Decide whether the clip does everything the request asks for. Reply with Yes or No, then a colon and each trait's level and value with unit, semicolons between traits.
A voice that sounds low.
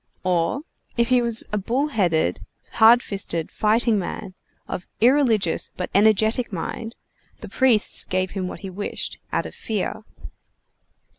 No: high, 215 Hz